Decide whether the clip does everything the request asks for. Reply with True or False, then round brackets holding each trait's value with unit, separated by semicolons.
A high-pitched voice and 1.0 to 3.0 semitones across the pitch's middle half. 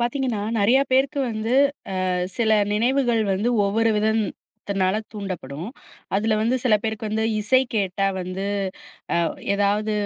True (215 Hz; 2.7 semitones)